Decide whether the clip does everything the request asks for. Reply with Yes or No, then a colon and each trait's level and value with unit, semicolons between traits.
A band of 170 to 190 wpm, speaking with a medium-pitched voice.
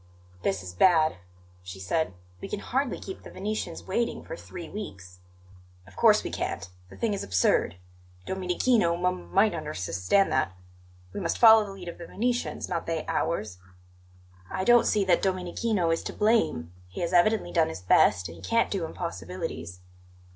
Yes: average, 175 wpm; medium, 175 Hz